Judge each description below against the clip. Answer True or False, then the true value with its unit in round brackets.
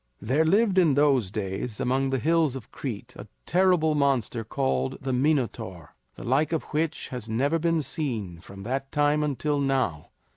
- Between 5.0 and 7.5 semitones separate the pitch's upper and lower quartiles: True (5.4 semitones)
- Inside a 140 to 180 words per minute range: True (170 wpm)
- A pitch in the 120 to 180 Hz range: True (135 Hz)